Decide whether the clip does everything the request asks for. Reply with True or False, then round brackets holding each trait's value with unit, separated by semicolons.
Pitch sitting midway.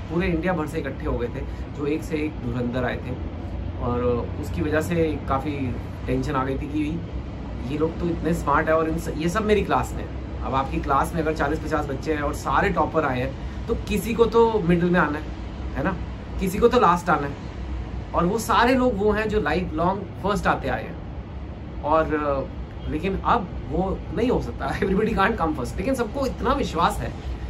True (150 Hz)